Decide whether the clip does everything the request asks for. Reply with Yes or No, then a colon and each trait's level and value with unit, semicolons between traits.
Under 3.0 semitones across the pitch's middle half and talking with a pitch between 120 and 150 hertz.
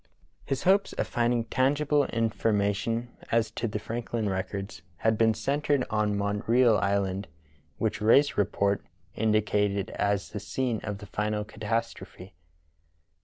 No: narrow, 2.5 semitones; low, 110 Hz